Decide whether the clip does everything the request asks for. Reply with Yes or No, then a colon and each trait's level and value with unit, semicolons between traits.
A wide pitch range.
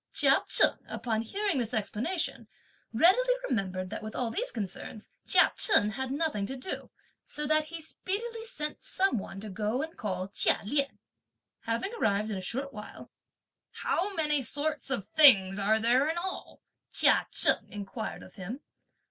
Yes: wide, 7.0 semitones